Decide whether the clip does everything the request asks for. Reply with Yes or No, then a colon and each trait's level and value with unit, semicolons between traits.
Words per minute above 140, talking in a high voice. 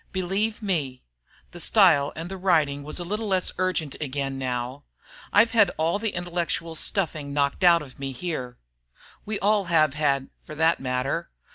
No: average, 165 wpm; medium, 165 Hz